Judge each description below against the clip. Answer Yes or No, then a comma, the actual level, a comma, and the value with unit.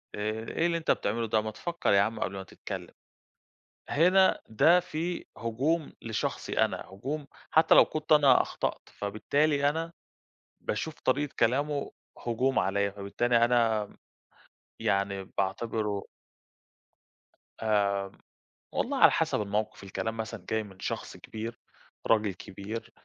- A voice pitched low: Yes, low, 115 Hz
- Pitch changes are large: Yes, wide, 6.0 semitones